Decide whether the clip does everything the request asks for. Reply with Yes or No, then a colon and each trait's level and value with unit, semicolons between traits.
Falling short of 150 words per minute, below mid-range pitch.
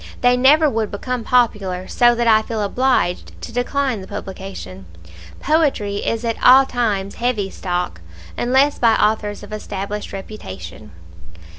No: average, 140 wpm; high, 220 Hz